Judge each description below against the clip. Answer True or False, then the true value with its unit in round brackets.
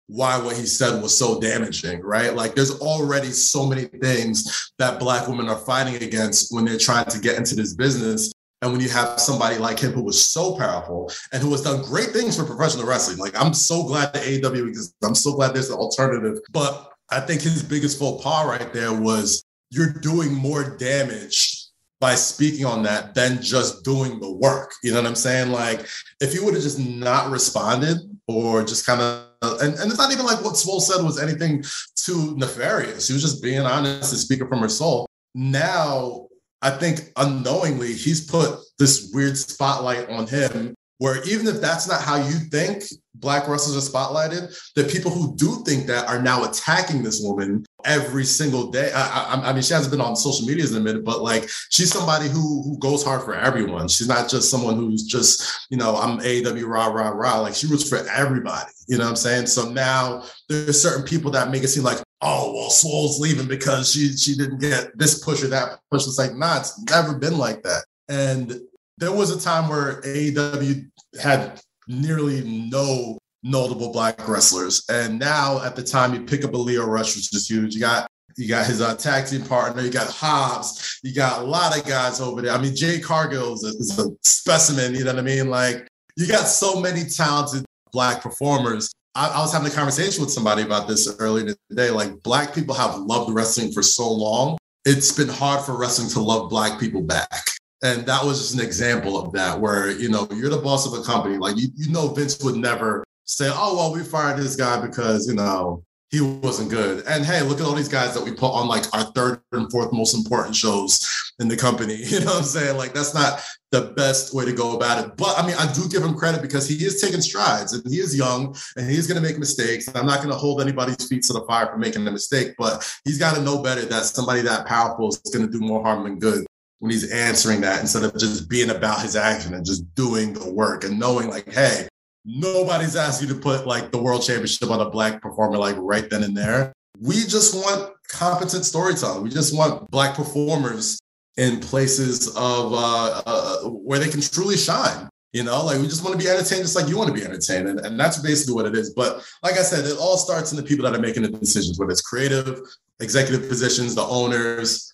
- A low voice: True (130 Hz)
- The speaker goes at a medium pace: False (220 wpm)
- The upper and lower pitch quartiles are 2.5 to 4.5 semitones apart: True (3.9 semitones)